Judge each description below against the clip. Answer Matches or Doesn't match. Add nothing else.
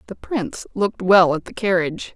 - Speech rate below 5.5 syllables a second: Doesn't match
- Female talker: Matches